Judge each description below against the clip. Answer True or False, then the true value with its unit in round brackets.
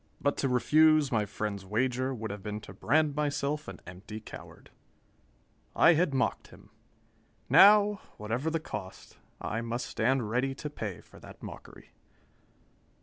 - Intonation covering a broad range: True (5.9 semitones)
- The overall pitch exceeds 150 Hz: False (130 Hz)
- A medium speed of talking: True (145 wpm)